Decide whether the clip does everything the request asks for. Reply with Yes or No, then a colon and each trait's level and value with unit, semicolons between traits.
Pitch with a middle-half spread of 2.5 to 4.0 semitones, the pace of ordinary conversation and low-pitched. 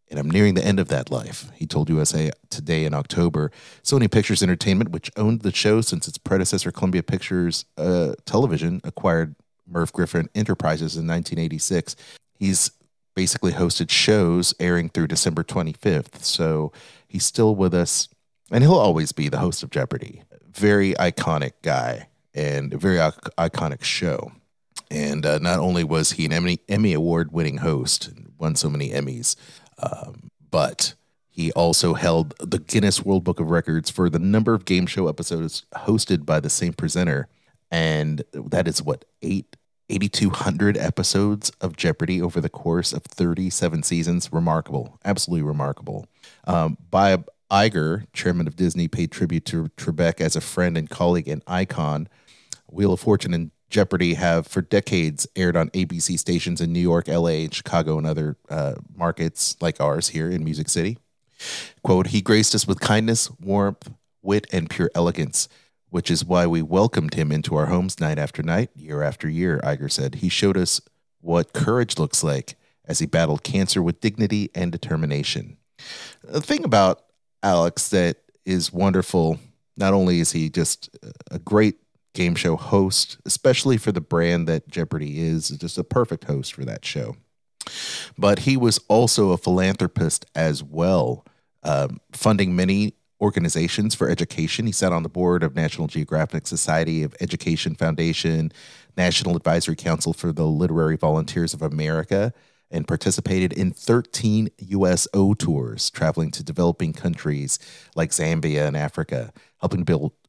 Yes: average, 3.5 semitones; average, 160 wpm; very low, 85 Hz